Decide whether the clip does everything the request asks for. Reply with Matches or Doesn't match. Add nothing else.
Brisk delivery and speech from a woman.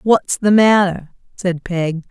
Doesn't match